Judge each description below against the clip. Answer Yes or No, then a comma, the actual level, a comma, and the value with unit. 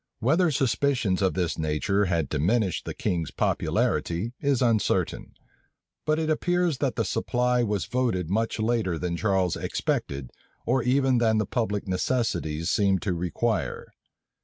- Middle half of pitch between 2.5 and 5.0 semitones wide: No, wide, 5.6 semitones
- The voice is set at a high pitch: No, low, 110 Hz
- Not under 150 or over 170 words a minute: No, average, 140 wpm